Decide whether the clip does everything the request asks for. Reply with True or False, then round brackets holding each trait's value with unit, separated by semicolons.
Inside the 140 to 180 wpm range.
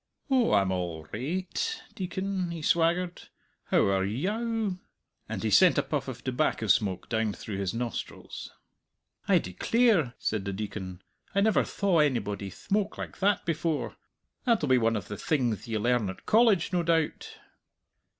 True (160 wpm)